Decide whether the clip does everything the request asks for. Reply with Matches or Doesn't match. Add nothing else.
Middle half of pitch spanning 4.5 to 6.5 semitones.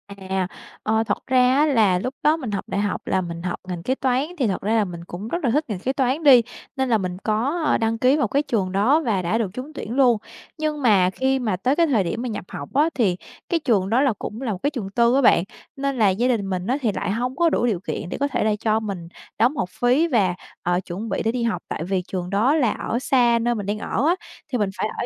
Matches